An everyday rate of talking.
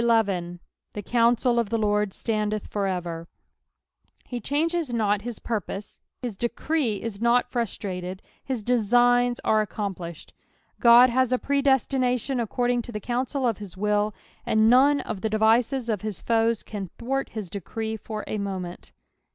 Yes: average, 150 wpm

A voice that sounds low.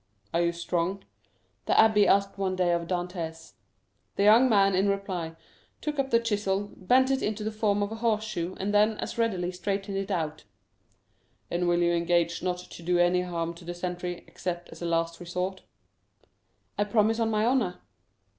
No: high, 190 Hz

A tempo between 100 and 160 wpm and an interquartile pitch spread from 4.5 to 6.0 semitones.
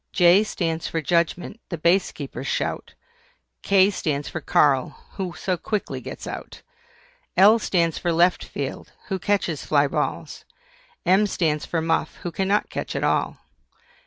No: average, 150 wpm; average, 3.1 semitones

